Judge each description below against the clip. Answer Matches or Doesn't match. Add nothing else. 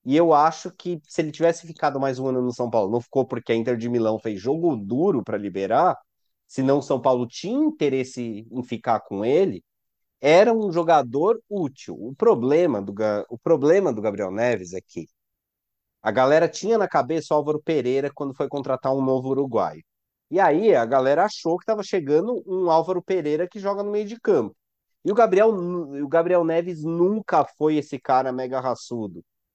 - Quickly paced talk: Matches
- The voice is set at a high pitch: Doesn't match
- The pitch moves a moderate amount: Doesn't match